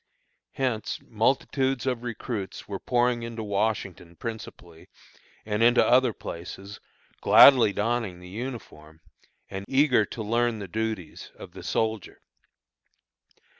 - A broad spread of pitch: No, average, 3.6 semitones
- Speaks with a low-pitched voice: Yes, low, 110 Hz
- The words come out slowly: Yes, slow, 115 wpm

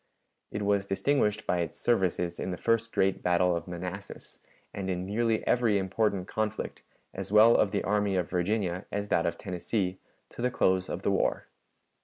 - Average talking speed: Yes, average, 180 wpm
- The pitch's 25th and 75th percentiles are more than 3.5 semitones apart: No, average, 3.0 semitones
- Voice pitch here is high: No, very low, 95 Hz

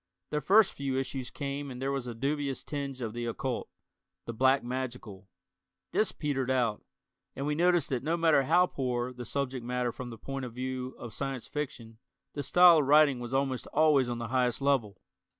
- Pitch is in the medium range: No, low, 130 Hz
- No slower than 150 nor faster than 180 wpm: No, average, 195 wpm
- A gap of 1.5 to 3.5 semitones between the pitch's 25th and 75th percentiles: Yes, narrow, 2.6 semitones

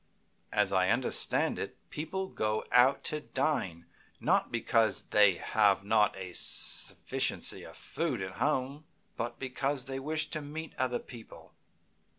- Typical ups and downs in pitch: No, wide, 5.7 semitones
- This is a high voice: No, low, 125 Hz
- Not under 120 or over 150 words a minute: Yes, average, 140 wpm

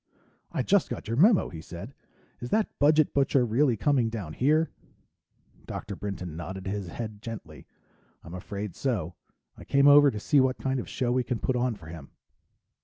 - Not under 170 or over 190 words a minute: Yes, average, 180 wpm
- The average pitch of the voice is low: Yes, low, 115 Hz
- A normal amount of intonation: No, wide, 6.2 semitones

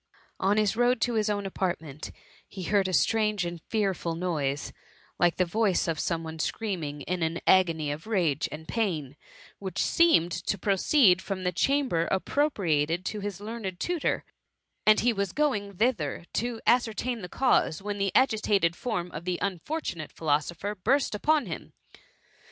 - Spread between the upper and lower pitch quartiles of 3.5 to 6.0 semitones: Yes, average, 4.7 semitones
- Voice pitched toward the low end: No, high, 190 Hz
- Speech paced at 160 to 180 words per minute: Yes, average, 165 wpm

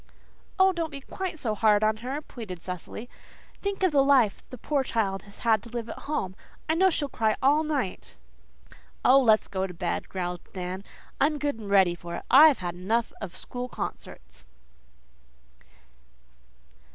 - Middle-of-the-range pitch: No, high, 230 Hz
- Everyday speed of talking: Yes, average, 165 wpm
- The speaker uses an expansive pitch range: Yes, wide, 6.8 semitones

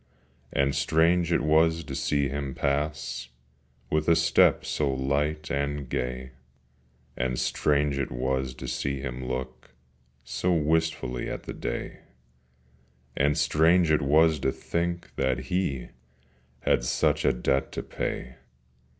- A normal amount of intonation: Yes, average, 3.1 semitones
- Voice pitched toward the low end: Yes, very low, 70 Hz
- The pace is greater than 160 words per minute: No, slow, 135 wpm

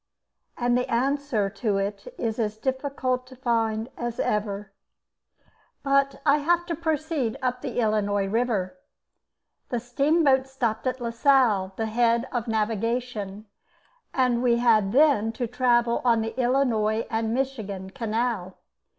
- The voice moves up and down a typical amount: Yes, average, 3.3 semitones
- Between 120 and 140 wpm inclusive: Yes, slow, 135 wpm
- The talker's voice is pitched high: Yes, high, 235 Hz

